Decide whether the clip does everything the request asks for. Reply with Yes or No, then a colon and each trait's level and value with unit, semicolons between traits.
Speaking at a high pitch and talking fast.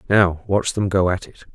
No: very low, 95 Hz; fast, 235 wpm